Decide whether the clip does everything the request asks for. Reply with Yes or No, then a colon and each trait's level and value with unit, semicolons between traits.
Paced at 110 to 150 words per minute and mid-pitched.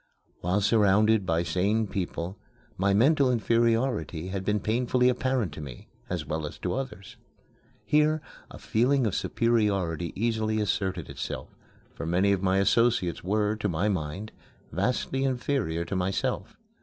No: average, 145 wpm; low, 105 Hz